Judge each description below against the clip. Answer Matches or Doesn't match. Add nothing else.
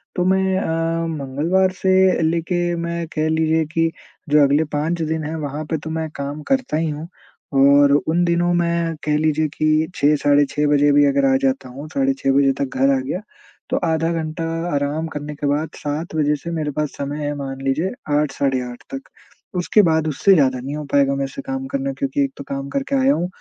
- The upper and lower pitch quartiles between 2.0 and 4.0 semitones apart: Matches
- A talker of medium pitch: Matches